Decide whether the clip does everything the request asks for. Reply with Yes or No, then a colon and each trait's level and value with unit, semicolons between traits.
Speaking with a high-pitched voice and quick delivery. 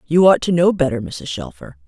No: low, 130 Hz; fast, 225 wpm